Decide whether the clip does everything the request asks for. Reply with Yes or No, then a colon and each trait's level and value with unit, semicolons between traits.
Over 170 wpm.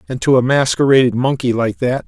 Yes: fast, 205 wpm